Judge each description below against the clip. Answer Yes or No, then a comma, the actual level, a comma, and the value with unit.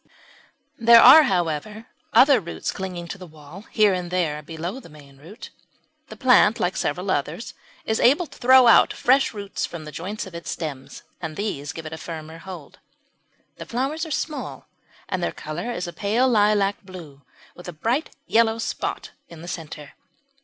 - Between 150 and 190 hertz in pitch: Yes, medium, 185 Hz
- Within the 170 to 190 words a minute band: Yes, average, 180 wpm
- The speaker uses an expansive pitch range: Yes, wide, 6.1 semitones